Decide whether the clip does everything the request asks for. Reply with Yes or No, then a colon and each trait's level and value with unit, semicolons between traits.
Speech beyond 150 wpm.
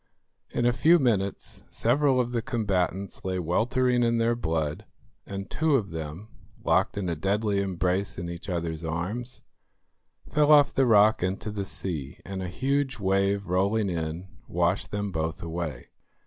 Yes: average, 160 wpm